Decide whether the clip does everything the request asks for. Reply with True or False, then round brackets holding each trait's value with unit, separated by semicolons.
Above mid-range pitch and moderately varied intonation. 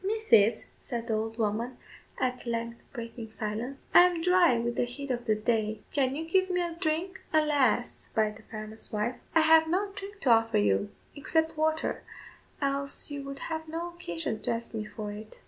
False (255 Hz; 6.3 semitones)